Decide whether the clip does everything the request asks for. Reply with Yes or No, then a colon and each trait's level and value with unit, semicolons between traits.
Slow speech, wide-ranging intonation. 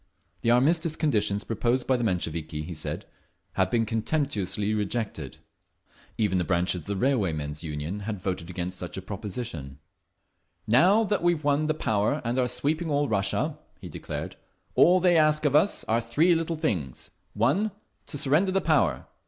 No: average, 165 wpm; wide, 8.3 semitones